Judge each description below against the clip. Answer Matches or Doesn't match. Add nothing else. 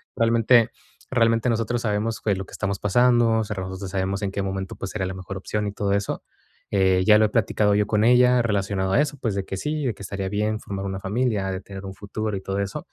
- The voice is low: Matches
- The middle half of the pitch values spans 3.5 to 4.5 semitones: Doesn't match